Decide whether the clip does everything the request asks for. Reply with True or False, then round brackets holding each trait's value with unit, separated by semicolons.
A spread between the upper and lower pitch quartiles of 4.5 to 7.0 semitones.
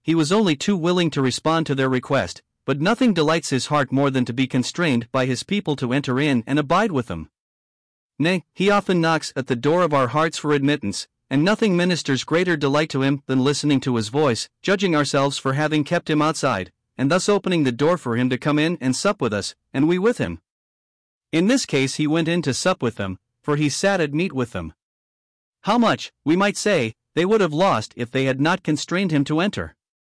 True (5.0 semitones)